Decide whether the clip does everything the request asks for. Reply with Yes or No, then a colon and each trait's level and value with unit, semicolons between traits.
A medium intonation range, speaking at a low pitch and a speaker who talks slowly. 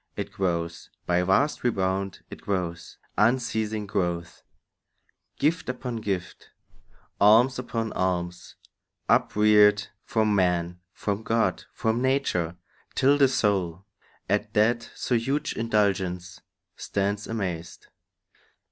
Yes: average, 4.1 semitones; low, 105 Hz; slow, 105 wpm